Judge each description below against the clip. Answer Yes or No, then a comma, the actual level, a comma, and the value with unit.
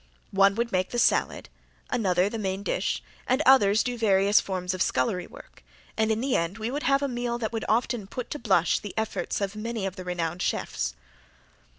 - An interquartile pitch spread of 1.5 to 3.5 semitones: No, average, 4.0 semitones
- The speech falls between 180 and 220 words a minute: Yes, fast, 205 wpm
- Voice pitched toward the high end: Yes, high, 210 Hz